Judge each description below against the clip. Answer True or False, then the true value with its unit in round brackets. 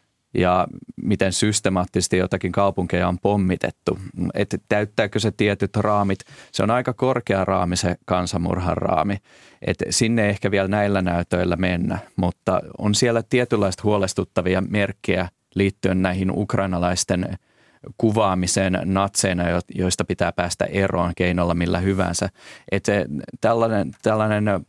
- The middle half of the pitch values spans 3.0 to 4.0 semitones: False (2.4 semitones)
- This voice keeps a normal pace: True (120 wpm)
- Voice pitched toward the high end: False (95 Hz)